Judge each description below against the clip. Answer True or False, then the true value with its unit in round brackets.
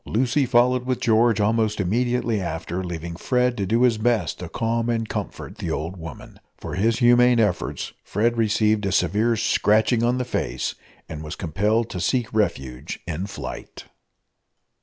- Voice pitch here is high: False (110 Hz)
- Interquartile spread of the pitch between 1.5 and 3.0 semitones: False (4.7 semitones)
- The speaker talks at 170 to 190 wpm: False (160 wpm)